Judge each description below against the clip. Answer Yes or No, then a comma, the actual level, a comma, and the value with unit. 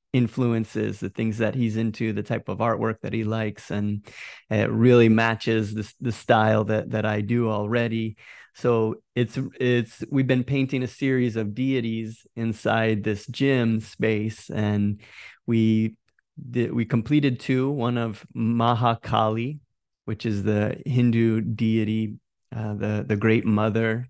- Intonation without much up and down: Yes, narrow, 1.8 semitones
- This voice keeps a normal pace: Yes, average, 145 wpm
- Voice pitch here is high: No, low, 115 Hz